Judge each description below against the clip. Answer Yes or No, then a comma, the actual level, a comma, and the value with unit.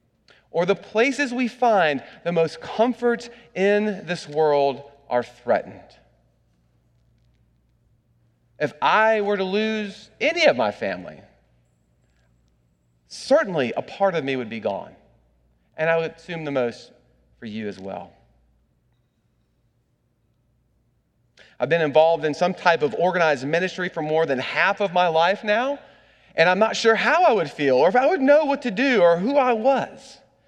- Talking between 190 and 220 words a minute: No, average, 150 wpm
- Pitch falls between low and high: Yes, medium, 165 Hz